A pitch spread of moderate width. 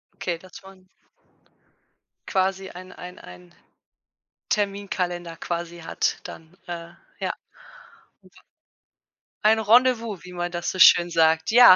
No: narrow, 2.2 semitones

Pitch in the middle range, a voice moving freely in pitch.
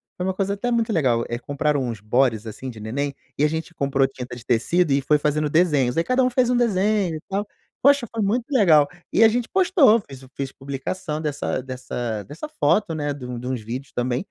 Yes: medium, 150 Hz; wide, 7.9 semitones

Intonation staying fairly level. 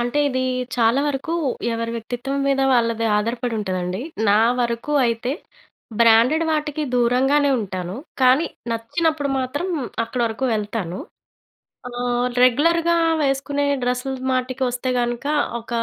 No: average, 3.1 semitones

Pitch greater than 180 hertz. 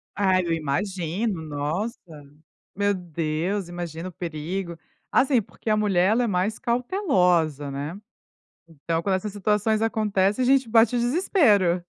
Yes: high, 190 Hz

